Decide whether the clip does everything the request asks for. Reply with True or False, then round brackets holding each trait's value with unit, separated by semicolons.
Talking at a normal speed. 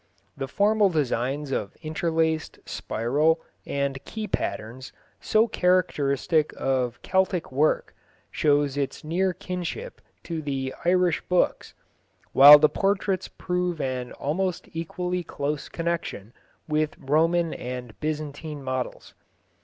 False (110 wpm)